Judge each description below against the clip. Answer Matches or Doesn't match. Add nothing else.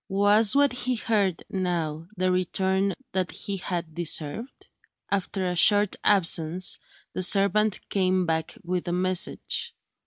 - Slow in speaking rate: Matches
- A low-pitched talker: Doesn't match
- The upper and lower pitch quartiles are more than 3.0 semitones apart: Doesn't match